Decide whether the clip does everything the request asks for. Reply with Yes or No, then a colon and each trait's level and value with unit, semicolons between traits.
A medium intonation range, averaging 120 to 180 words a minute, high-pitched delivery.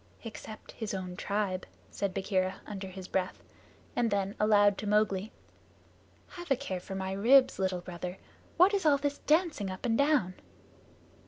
Yes: average, 4.6 semitones; average, 160 wpm; high, 205 Hz